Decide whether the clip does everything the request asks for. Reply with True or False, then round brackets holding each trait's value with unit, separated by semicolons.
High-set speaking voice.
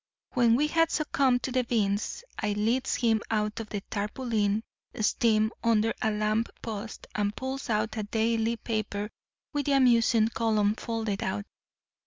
True (225 Hz)